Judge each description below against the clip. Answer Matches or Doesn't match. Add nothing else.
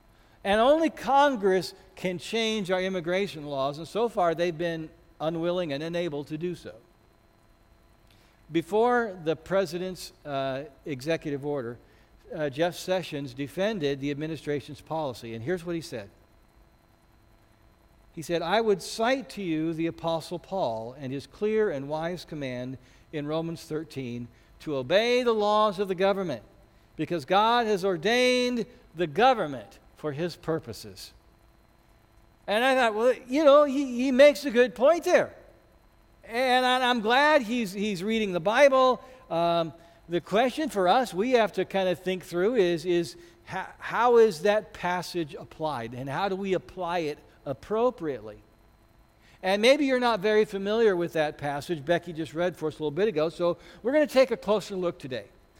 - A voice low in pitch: Doesn't match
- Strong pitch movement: Matches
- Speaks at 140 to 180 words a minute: Matches